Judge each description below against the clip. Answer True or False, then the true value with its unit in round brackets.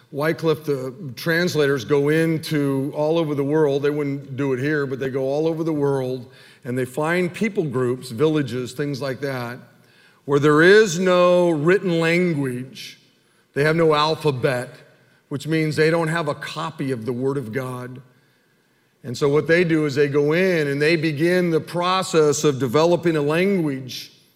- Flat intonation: False (3.0 semitones)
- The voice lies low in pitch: False (150 Hz)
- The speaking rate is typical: True (170 wpm)